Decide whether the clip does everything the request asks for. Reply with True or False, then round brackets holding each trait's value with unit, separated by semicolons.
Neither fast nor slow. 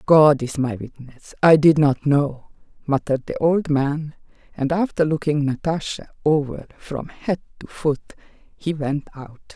True (150 wpm)